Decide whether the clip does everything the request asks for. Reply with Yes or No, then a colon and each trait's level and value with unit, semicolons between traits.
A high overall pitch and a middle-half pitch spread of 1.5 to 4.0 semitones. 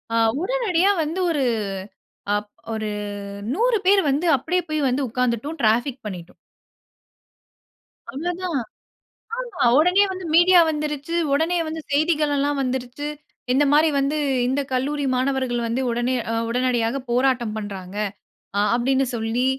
No: very high, 275 Hz; average, 4.9 semitones